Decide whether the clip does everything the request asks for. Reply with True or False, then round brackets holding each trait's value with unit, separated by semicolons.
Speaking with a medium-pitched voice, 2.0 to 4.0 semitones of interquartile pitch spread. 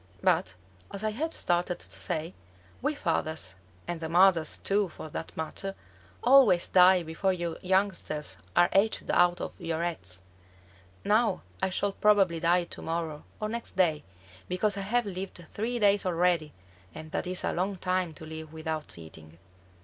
True (180 Hz; 3.7 semitones)